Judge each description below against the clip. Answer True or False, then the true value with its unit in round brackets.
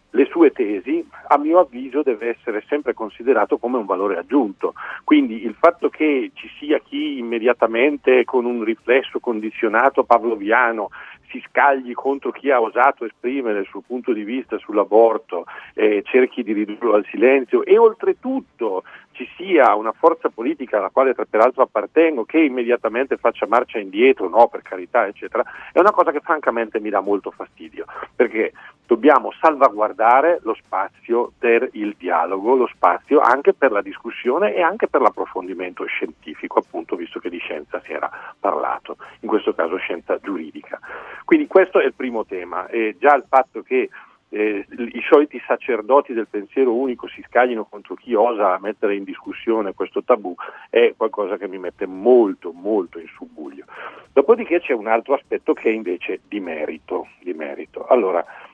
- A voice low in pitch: False (165 Hz)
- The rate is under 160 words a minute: False (165 wpm)